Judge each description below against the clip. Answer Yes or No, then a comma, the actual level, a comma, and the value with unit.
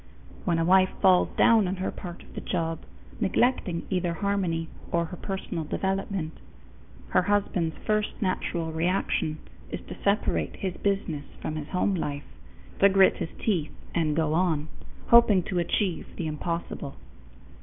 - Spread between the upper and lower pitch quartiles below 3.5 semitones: Yes, average, 3.1 semitones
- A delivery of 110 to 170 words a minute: Yes, average, 150 wpm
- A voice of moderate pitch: Yes, medium, 180 Hz